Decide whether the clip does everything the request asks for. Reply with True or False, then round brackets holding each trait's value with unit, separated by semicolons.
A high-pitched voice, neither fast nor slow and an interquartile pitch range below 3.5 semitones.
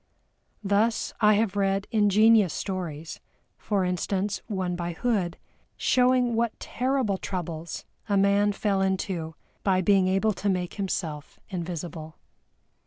False (195 Hz; 125 wpm; 2.9 semitones)